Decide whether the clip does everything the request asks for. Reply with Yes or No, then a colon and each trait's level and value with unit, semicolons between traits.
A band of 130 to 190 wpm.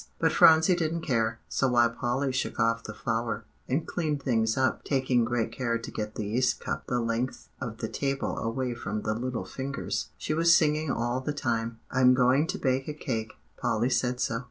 No: average, 200 wpm